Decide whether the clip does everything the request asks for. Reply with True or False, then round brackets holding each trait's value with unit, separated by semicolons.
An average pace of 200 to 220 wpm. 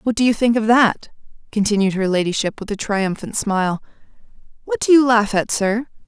False (190 wpm)